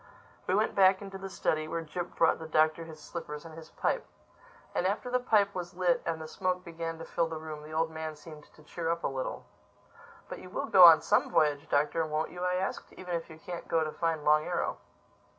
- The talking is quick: Yes, fast, 230 wpm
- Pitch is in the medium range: Yes, medium, 165 Hz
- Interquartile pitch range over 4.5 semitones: No, narrow, 2.5 semitones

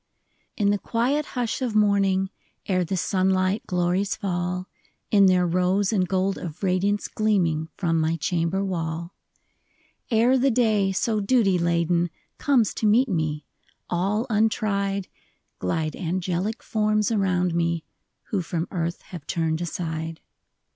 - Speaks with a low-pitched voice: No, high, 190 Hz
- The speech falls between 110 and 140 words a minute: Yes, slow, 135 wpm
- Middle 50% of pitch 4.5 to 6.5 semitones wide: No, average, 3.6 semitones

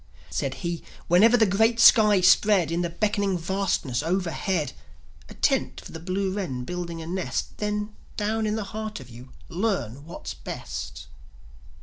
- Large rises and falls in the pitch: No, average, 4.0 semitones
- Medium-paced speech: Yes, average, 155 wpm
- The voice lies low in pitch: No, medium, 185 Hz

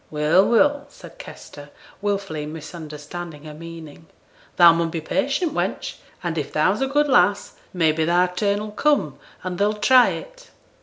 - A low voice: No, medium, 175 Hz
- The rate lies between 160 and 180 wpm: Yes, average, 165 wpm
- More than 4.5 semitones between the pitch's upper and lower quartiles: Yes, average, 5.1 semitones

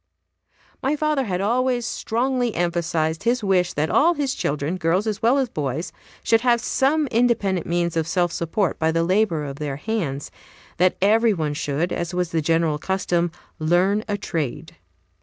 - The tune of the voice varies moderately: No, wide, 5.7 semitones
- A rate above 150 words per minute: Yes, average, 170 wpm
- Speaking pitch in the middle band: Yes, medium, 180 Hz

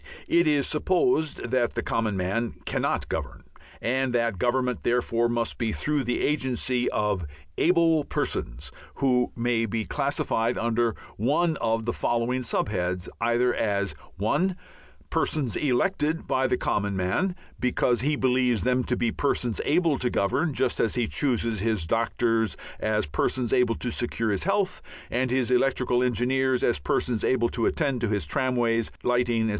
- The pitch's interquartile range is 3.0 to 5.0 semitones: No, narrow, 2.6 semitones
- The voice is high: No, low, 120 Hz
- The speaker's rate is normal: Yes, average, 155 wpm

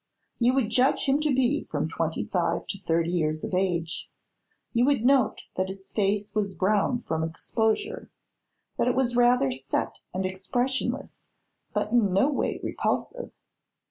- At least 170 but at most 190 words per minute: No, average, 155 wpm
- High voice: Yes, high, 215 Hz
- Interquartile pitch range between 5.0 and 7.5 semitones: Yes, wide, 5.4 semitones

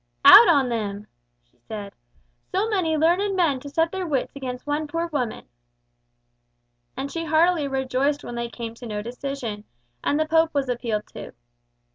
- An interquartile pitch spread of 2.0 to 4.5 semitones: No, wide, 5.4 semitones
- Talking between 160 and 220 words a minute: Yes, average, 165 wpm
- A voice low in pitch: No, very high, 280 Hz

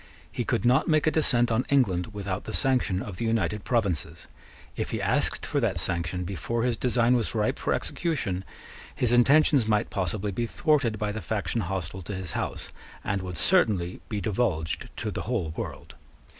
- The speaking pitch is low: Yes, low, 110 Hz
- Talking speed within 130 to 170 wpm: No, average, 185 wpm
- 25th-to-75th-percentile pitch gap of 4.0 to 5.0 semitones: Yes, average, 4.6 semitones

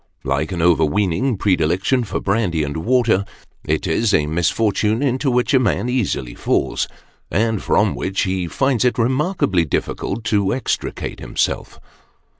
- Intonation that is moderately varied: No, wide, 6.0 semitones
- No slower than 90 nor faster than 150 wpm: Yes, average, 145 wpm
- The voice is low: Yes, low, 100 Hz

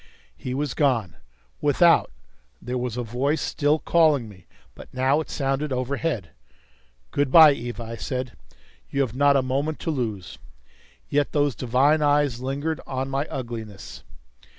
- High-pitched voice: No, low, 135 Hz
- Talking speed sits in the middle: Yes, average, 150 wpm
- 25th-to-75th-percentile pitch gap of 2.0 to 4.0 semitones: Yes, average, 3.0 semitones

